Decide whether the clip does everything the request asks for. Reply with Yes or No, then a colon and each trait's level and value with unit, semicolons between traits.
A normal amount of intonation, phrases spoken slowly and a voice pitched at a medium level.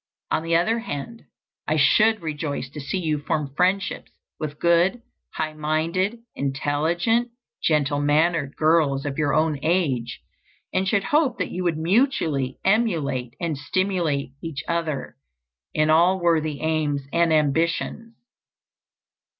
Yes: average, 4.0 semitones; slow, 130 wpm; medium, 160 Hz